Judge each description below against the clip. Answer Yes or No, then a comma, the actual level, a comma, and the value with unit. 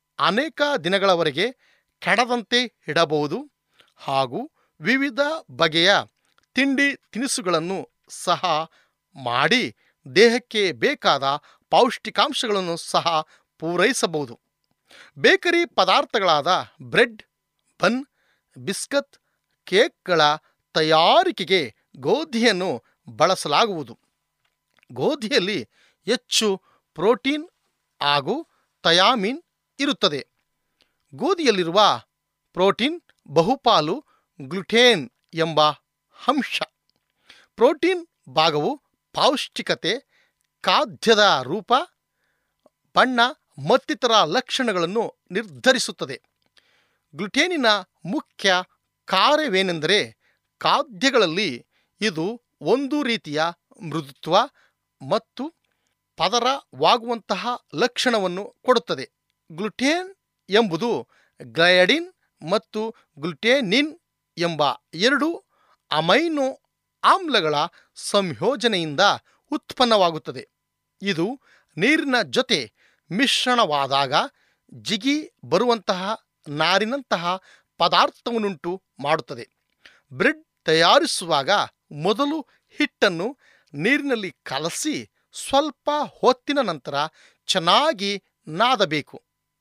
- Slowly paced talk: Yes, slow, 60 wpm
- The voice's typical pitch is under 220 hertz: No, high, 225 Hz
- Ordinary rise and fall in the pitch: No, wide, 7.8 semitones